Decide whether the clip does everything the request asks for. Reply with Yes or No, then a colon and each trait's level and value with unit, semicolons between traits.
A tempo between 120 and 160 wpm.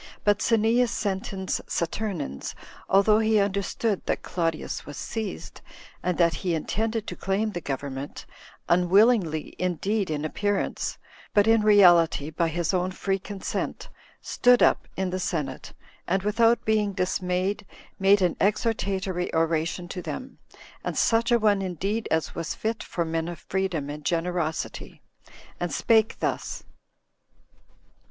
Yes: slow, 135 wpm